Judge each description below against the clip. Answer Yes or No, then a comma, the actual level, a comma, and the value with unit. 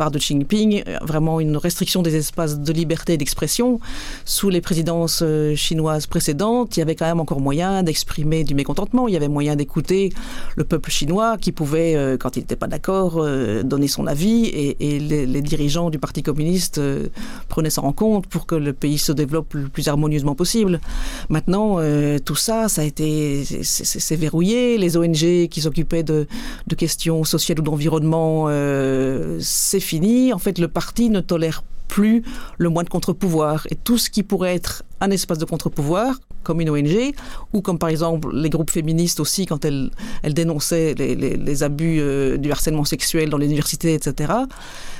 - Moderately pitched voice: Yes, medium, 160 Hz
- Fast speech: No, average, 190 wpm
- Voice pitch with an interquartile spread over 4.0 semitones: No, average, 3.3 semitones